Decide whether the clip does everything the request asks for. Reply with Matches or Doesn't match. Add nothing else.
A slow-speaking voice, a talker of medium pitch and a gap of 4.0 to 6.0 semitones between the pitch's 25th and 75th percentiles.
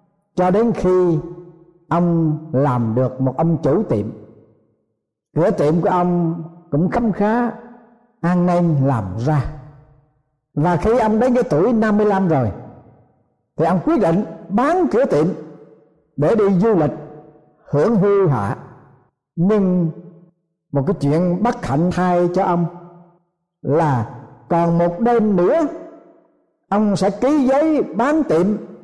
Matches